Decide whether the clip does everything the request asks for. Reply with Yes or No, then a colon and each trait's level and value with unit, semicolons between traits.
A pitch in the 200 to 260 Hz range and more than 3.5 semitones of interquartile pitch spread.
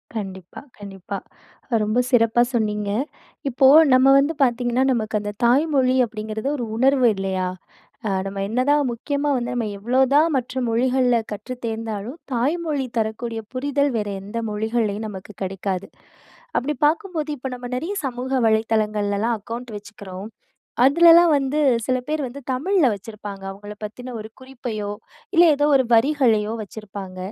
Yes: high, 235 Hz; average, 4.0 semitones